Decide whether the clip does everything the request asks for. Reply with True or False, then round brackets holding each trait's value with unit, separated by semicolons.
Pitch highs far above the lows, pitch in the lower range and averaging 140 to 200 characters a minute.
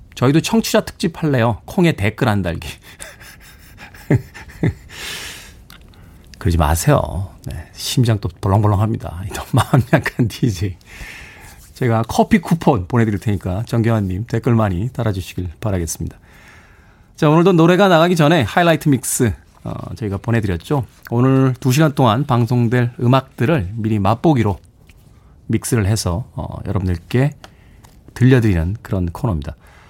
False (6.0 semitones; 110 Hz; 285 characters per minute)